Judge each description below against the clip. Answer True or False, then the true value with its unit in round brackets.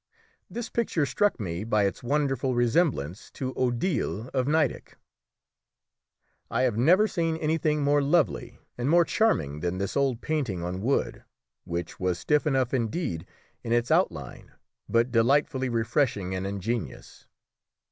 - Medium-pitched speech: False (130 Hz)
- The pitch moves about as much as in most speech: False (6.3 semitones)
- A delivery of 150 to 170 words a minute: False (135 wpm)